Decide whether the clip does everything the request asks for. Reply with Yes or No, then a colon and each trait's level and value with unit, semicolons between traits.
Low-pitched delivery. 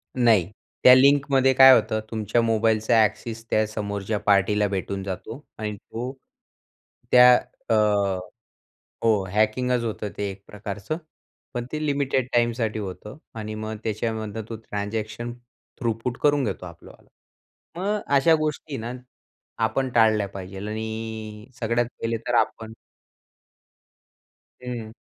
Yes: low, 110 Hz